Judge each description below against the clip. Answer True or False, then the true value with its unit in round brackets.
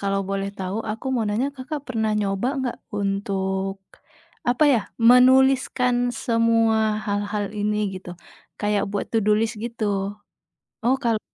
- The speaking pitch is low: False (220 Hz)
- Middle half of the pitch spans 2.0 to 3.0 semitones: False (3.5 semitones)